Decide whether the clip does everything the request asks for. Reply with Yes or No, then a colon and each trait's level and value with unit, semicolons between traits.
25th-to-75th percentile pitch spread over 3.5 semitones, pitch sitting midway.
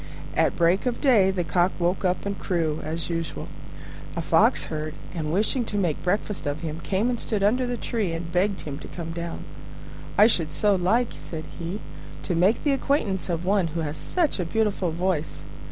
Yes: average, 3.9 semitones; medium, 180 Hz